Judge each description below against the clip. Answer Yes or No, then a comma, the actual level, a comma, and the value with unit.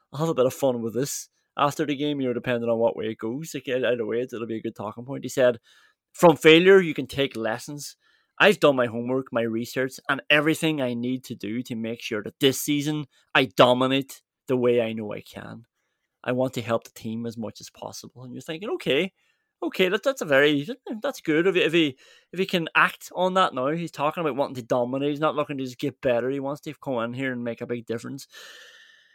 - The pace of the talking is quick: Yes, fast, 240 wpm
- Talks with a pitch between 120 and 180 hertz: Yes, low, 135 Hz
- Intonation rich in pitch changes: No, average, 4.6 semitones